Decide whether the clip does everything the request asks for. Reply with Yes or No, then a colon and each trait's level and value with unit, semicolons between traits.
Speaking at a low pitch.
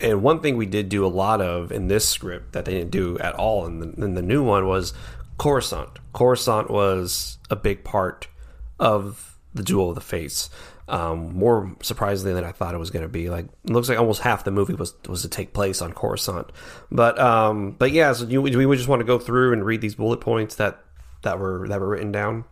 Yes: low, 105 Hz